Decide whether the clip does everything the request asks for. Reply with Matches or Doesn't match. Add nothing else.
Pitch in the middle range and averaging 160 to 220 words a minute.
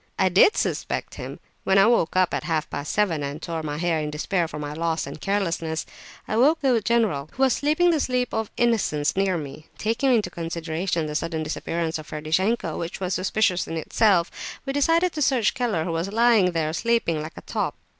Matches